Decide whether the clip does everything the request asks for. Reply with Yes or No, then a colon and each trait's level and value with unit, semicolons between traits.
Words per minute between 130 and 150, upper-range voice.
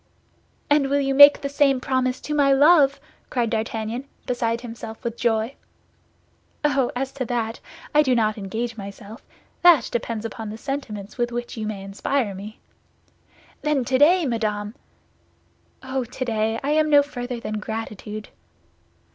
Yes: average, 145 wpm; high, 240 Hz